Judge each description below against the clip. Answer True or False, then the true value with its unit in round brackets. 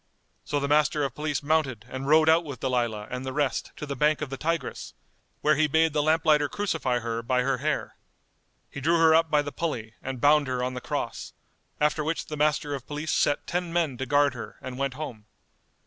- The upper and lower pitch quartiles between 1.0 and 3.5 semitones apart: True (3.1 semitones)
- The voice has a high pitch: False (145 Hz)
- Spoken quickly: True (225 wpm)